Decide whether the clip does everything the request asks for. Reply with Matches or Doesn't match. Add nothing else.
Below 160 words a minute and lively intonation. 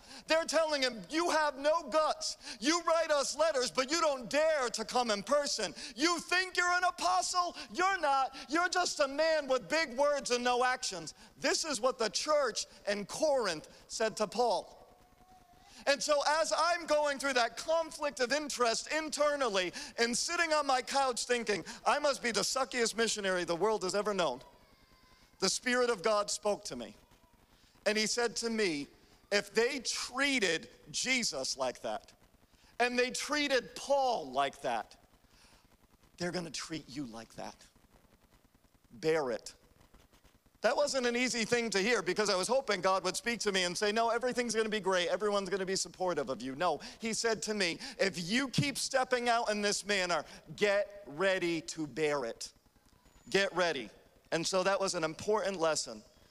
Doesn't match